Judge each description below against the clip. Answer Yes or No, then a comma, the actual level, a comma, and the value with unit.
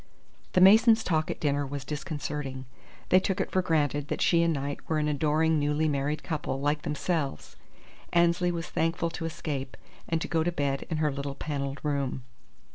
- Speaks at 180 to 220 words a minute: Yes, average, 185 wpm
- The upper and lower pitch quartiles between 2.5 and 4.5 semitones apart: Yes, average, 2.8 semitones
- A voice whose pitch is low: No, medium, 150 Hz